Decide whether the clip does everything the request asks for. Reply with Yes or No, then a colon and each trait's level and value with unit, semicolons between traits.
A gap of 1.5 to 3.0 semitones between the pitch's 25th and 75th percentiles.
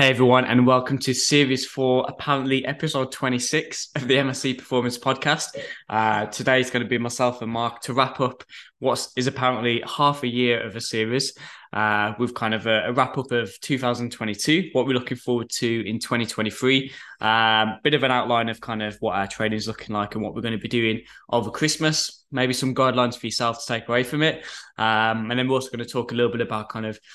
Yes: narrow, 2.6 semitones